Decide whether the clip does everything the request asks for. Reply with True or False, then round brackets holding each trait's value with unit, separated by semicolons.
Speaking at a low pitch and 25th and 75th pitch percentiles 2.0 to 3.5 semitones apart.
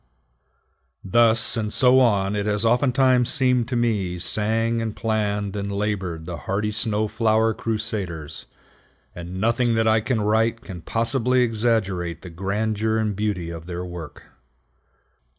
True (110 Hz; 2.9 semitones)